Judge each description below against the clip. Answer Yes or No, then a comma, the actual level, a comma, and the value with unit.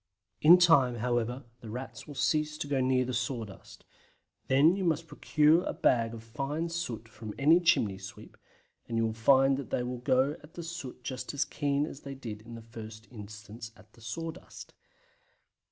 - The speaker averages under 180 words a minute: No, average, 185 wpm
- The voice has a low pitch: Yes, low, 130 Hz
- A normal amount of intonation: Yes, average, 4.7 semitones